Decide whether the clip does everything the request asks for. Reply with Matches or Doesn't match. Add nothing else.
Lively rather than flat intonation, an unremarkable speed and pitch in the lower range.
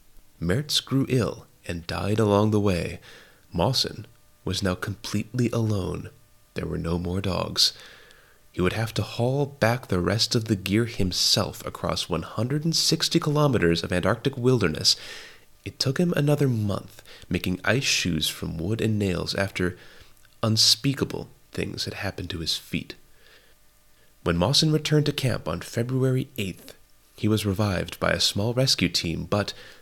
Matches